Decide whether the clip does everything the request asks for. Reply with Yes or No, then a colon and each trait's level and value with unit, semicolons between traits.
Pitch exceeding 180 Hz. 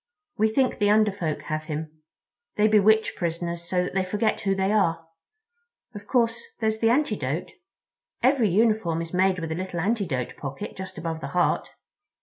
Yes: high, 190 Hz